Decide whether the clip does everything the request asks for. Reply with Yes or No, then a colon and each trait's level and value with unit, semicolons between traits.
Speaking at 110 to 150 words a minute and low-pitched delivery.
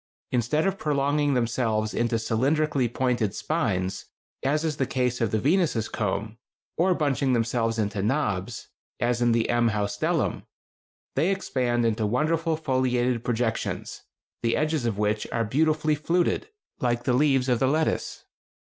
Yes: average, 145 wpm; low, 125 Hz